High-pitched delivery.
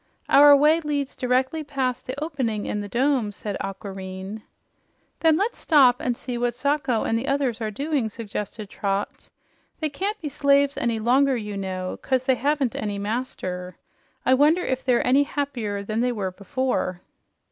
Yes: very high, 250 Hz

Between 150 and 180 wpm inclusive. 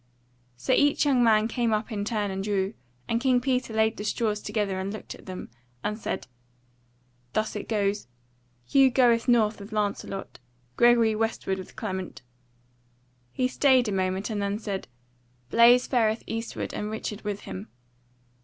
Yes: average, 160 wpm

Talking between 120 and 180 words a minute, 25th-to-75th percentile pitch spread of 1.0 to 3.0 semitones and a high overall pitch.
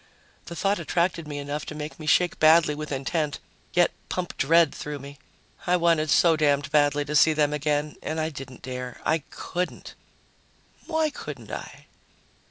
No: average, 170 wpm; narrow, 2.6 semitones; medium, 155 Hz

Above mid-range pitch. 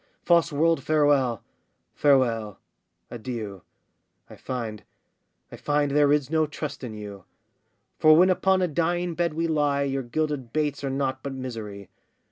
No: medium, 140 Hz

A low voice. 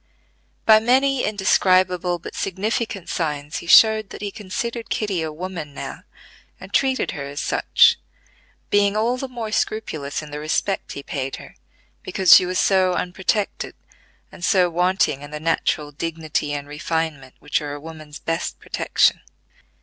No: medium, 180 Hz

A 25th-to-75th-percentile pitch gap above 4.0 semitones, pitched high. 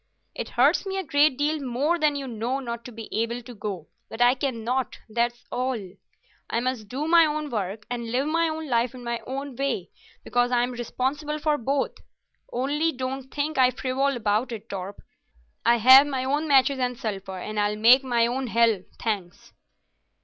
No: average, 3.2 semitones; very high, 250 Hz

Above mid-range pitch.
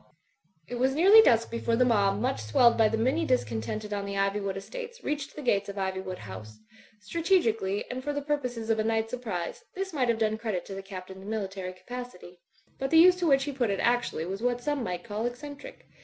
Yes: high, 225 Hz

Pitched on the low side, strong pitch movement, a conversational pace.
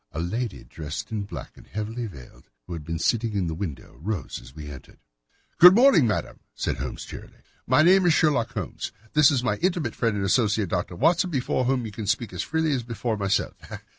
No: low, 115 Hz; wide, 7.0 semitones; fast, 210 wpm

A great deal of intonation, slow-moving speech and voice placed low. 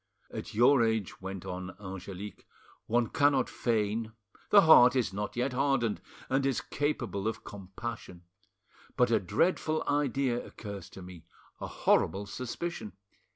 No: average, 5.0 semitones; slow, 125 wpm; low, 115 Hz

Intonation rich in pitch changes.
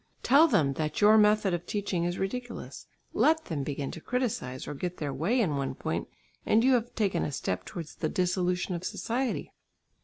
Yes: wide, 6.4 semitones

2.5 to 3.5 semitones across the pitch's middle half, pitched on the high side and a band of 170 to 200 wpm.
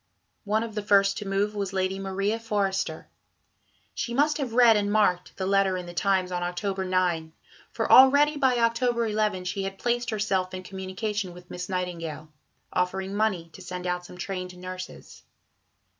Yes: average, 2.8 semitones; high, 195 Hz; average, 175 wpm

